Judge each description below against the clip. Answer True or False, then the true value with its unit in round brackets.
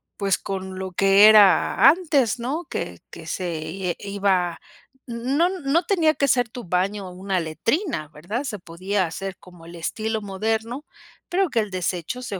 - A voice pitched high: True (200 Hz)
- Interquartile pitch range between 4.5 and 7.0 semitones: True (5.5 semitones)